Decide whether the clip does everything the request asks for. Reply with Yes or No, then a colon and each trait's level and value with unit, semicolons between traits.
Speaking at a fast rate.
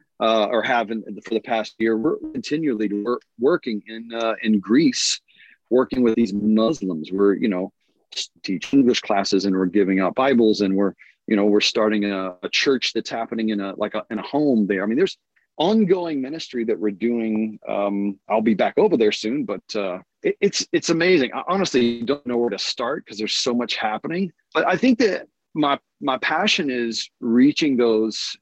No: average, 195 wpm